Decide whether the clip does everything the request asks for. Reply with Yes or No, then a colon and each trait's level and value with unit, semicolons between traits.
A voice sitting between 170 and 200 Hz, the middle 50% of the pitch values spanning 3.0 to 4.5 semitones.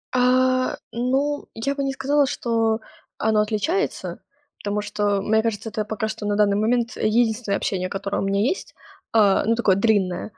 No: high, 220 Hz; average, 3.4 semitones